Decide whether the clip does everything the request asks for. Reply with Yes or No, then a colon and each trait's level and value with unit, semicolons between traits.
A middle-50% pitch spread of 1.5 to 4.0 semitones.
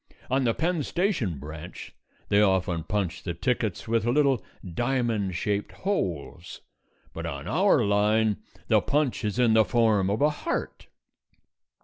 No: average, 5.0 semitones